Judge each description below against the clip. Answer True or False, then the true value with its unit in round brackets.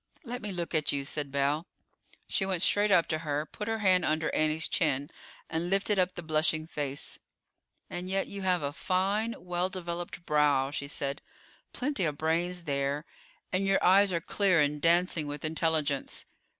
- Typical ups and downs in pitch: True (3.9 semitones)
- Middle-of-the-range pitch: True (165 Hz)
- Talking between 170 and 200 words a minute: True (175 wpm)